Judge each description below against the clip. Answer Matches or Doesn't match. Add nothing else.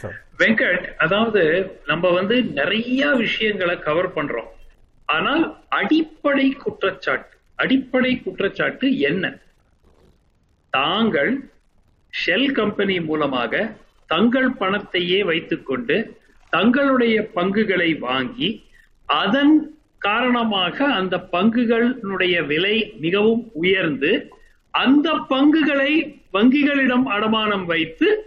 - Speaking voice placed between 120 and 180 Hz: Doesn't match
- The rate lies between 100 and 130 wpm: Doesn't match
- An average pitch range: Doesn't match